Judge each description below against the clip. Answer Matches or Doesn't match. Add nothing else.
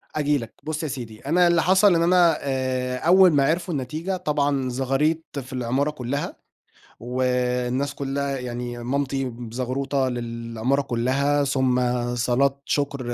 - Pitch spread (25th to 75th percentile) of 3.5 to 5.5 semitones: Doesn't match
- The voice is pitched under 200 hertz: Matches